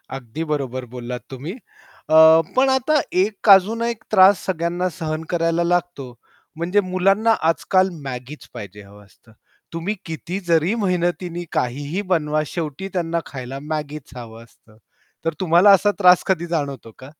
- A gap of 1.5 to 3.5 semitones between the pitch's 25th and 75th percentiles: No, wide, 5.4 semitones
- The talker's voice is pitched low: No, medium, 165 Hz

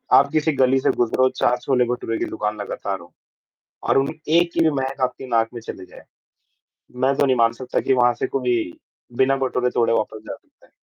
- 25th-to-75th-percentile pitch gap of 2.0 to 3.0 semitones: Yes, narrow, 2.5 semitones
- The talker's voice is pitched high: No, low, 125 Hz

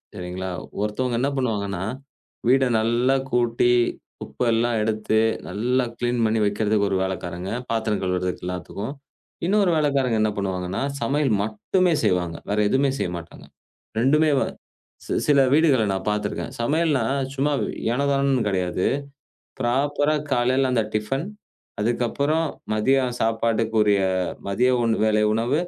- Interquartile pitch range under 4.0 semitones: No, average, 4.7 semitones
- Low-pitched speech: Yes, low, 115 Hz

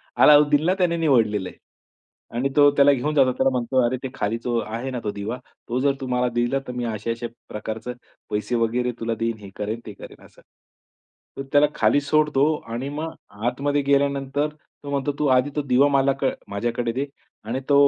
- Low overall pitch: Yes, low, 130 Hz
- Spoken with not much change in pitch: No, average, 3.6 semitones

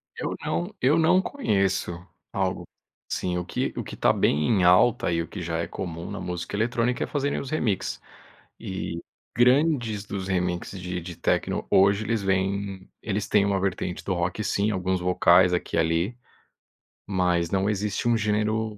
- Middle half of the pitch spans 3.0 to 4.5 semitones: Yes, average, 3.3 semitones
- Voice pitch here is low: Yes, very low, 95 Hz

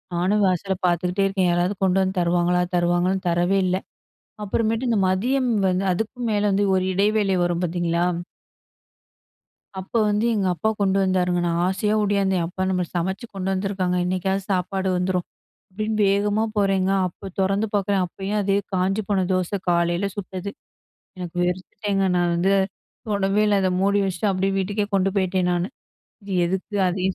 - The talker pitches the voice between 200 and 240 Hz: No, high, 190 Hz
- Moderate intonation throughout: No, narrow, 1.9 semitones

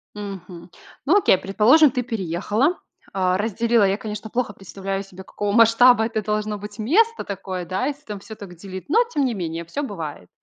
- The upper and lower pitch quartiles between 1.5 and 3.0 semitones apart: No, average, 4.0 semitones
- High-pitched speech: Yes, high, 210 Hz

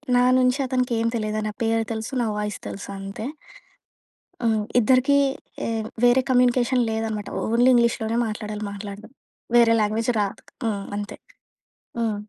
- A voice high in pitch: Yes, high, 225 Hz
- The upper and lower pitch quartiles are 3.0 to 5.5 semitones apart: No, narrow, 2.5 semitones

